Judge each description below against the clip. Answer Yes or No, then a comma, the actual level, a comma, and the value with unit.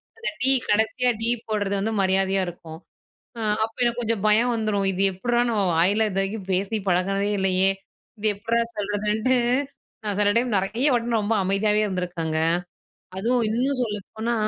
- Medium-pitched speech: No, high, 210 Hz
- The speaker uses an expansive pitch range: No, average, 3.0 semitones